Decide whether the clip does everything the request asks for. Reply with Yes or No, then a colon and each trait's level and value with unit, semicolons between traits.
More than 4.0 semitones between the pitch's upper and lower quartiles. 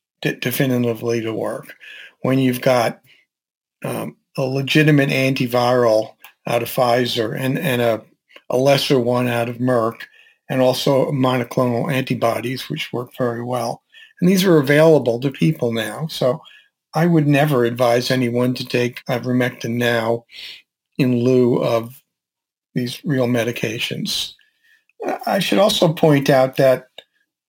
No: average, 3.3 semitones